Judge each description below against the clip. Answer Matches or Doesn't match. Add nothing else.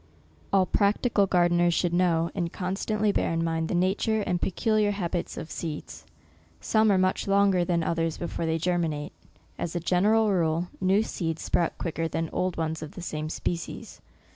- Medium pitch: Matches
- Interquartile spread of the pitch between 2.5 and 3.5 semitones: Matches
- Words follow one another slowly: Doesn't match